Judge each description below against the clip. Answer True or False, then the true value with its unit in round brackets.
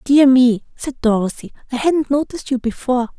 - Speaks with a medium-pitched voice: False (255 Hz)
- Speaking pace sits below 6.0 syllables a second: True (5.6 syllables/s)